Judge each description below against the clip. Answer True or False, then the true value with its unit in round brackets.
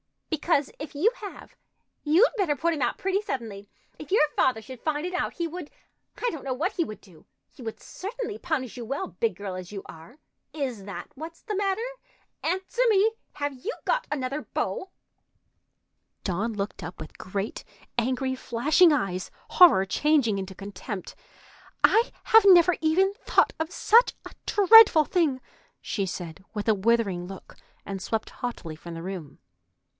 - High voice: True (275 Hz)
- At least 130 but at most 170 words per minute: True (165 wpm)